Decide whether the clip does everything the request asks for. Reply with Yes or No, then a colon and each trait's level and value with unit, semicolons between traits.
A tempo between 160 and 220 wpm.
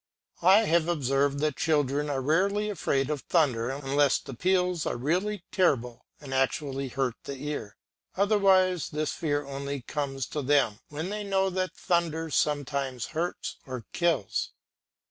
No: average, 145 wpm